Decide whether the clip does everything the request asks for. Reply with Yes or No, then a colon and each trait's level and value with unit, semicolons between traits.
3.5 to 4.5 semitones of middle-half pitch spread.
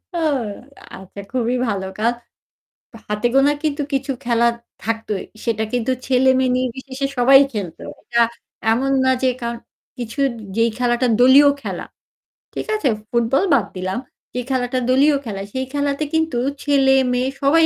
No: average, 2.8 semitones